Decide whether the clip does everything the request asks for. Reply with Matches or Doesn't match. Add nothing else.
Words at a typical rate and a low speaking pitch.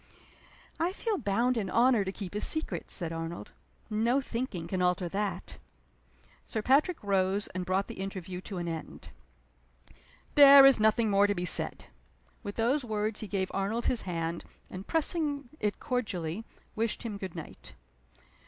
Doesn't match